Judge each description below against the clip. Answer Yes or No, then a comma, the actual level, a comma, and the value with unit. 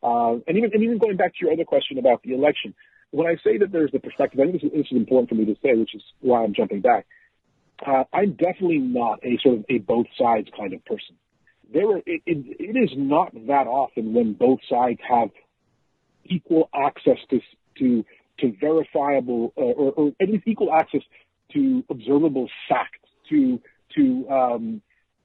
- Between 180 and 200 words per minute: Yes, average, 195 wpm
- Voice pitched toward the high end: No, medium, 160 Hz